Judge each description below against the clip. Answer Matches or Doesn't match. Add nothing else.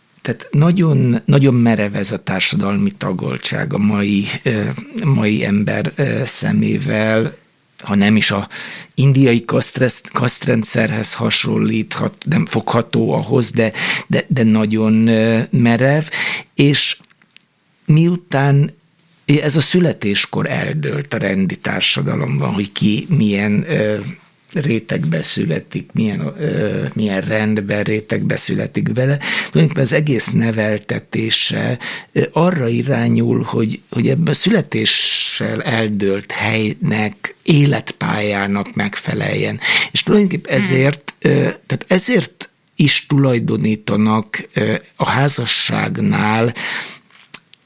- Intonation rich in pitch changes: Matches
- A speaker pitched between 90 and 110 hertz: Doesn't match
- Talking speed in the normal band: Doesn't match